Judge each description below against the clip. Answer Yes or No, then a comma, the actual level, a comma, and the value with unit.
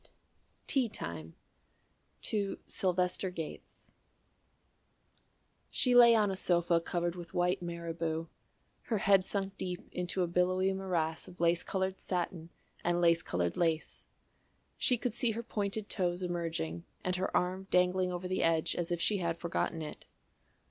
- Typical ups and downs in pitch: No, narrow, 2.2 semitones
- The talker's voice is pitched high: No, medium, 180 Hz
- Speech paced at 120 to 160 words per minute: Yes, average, 150 wpm